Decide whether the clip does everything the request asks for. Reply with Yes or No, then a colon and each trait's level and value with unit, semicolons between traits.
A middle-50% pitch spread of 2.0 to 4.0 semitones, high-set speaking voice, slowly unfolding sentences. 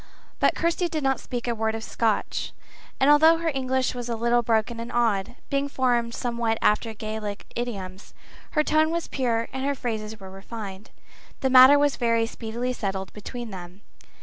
No: average, 3.2 semitones; high, 235 Hz; average, 175 wpm